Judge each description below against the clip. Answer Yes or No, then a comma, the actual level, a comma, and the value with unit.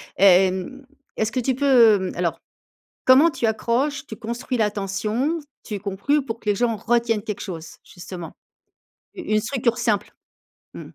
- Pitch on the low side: No, high, 225 Hz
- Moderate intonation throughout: Yes, average, 4.2 semitones